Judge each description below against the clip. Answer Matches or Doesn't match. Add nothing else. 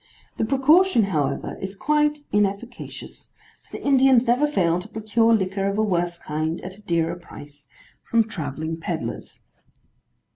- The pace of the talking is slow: Doesn't match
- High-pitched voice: Matches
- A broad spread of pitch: Matches